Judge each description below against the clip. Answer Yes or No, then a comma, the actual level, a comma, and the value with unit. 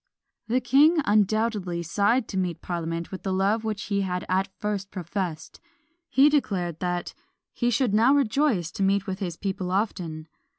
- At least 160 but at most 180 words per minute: Yes, average, 165 wpm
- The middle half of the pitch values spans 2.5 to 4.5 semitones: Yes, average, 3.6 semitones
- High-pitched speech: Yes, high, 195 Hz